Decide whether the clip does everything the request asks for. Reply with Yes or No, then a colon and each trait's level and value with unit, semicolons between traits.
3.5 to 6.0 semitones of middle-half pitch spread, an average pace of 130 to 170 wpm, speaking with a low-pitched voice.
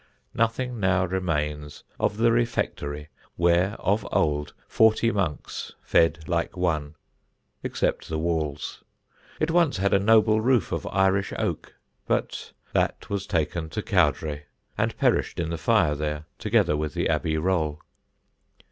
Yes: average, 5.2 semitones; average, 140 wpm; very low, 85 Hz